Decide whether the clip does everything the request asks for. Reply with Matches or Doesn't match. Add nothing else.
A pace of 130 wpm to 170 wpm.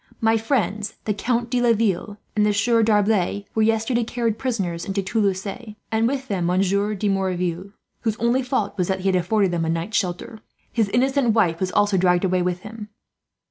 Doesn't match